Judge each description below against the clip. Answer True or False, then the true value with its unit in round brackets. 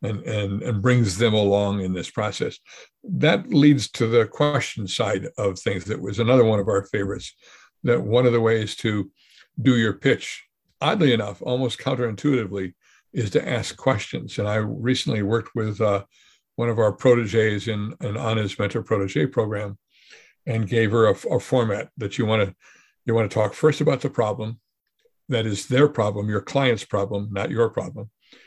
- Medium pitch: False (110 Hz)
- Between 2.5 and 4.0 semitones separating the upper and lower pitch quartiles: True (3.2 semitones)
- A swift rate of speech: False (180 wpm)